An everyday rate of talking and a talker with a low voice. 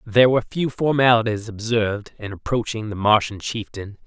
Yes: average, 145 wpm; low, 110 Hz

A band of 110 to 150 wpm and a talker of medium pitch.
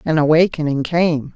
Yes: slow, 135 wpm; medium, 155 Hz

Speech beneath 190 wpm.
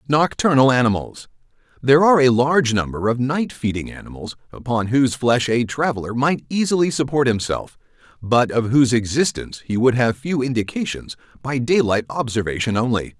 Yes: average, 145 wpm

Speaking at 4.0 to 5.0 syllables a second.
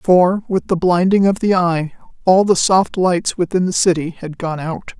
Yes: 4.5 syllables/s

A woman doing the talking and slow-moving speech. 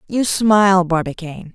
Yes: female; slow, 115 wpm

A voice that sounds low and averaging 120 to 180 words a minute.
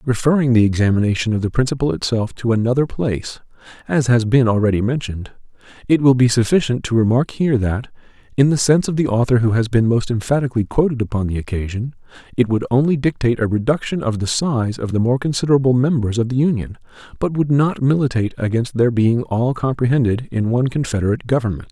No: low, 120 Hz; average, 190 wpm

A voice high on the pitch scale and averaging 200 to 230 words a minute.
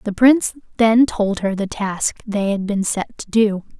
Yes: high, 210 Hz; fast, 205 wpm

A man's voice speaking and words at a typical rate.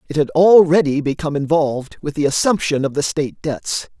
Yes: male; average, 180 wpm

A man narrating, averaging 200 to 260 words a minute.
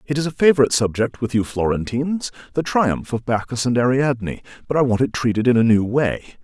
Yes: male; fast, 205 wpm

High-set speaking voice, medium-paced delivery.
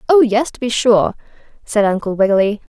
Yes: high, 225 Hz; average, 175 wpm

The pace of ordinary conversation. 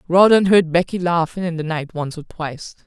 No: fast, 210 wpm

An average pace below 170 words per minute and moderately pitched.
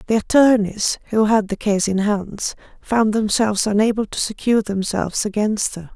No: average, 160 wpm; high, 210 Hz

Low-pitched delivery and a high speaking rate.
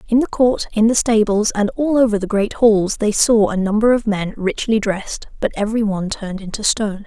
No: high, 215 Hz; fast, 220 wpm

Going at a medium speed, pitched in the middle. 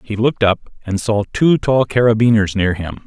No: average, 195 wpm; low, 110 Hz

